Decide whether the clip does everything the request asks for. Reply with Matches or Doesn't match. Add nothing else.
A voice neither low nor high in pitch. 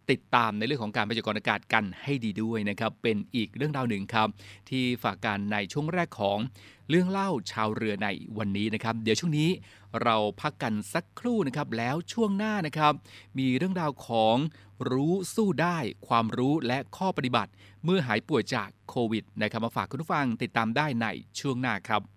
Doesn't match